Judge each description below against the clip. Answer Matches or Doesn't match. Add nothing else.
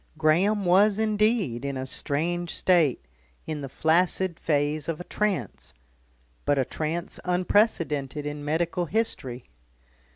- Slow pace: Matches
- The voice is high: Doesn't match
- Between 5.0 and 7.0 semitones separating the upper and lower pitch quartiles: Doesn't match